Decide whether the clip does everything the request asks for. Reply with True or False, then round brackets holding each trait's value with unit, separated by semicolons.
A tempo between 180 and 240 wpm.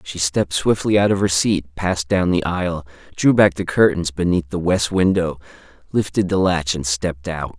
True (200 wpm)